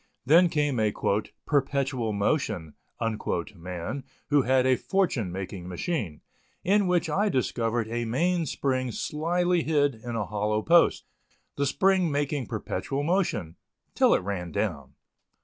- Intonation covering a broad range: Yes, wide, 7.2 semitones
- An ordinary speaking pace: No, slow, 130 wpm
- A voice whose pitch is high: No, low, 130 Hz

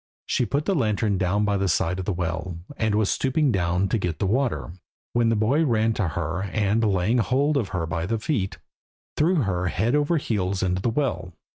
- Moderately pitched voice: No, low, 105 Hz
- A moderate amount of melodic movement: Yes, average, 4.8 semitones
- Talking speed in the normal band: No, fast, 210 wpm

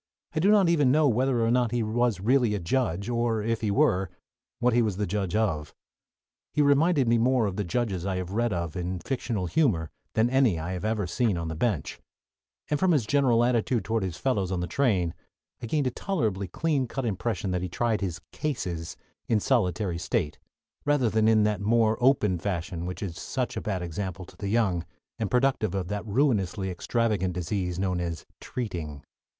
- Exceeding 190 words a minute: Yes, average, 200 wpm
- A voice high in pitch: No, low, 105 Hz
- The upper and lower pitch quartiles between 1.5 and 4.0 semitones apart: No, average, 5.1 semitones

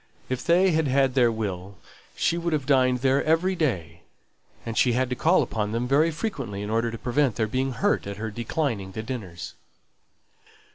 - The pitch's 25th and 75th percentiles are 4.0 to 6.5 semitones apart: Yes, wide, 5.4 semitones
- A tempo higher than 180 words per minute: Yes, average, 190 wpm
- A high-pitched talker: No, low, 125 Hz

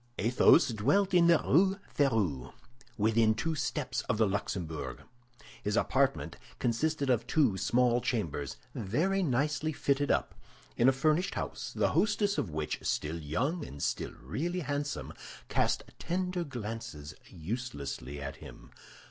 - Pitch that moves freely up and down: Yes, wide, 8.1 semitones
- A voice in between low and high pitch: No, low, 125 Hz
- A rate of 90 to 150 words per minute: Yes, slow, 135 wpm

